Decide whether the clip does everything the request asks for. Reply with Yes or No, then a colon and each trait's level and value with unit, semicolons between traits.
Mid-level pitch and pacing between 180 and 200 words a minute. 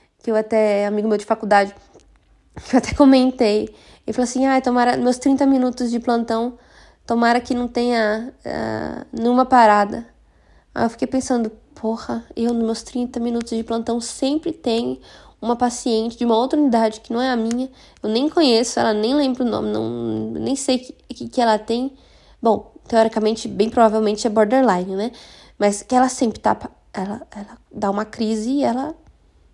No: high, 235 Hz; fast, 185 wpm